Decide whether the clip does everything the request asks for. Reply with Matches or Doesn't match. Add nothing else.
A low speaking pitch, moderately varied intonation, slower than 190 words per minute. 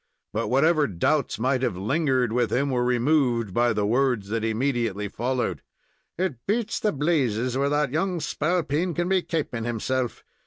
Matches